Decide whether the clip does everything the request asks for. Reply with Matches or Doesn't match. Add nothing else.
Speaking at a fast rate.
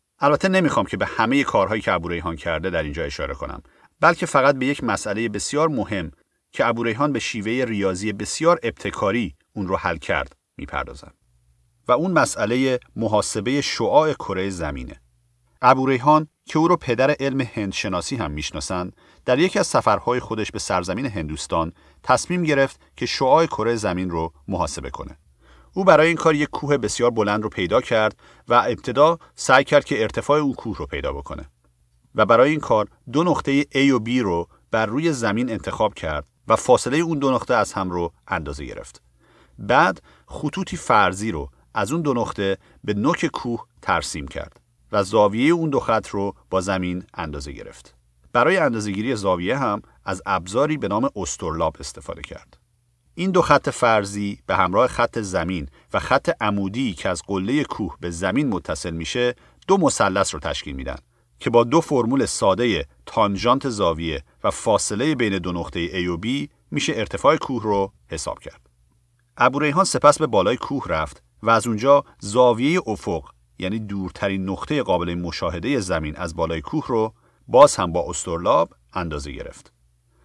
Matches